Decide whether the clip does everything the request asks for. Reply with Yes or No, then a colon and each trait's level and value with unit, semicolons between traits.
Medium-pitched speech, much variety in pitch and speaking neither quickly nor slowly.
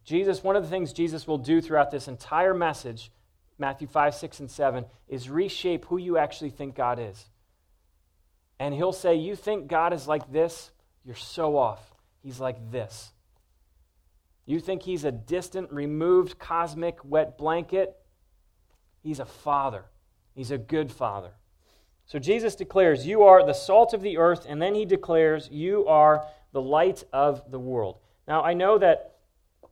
Yes: medium, 145 Hz; wide, 7.2 semitones; average, 165 wpm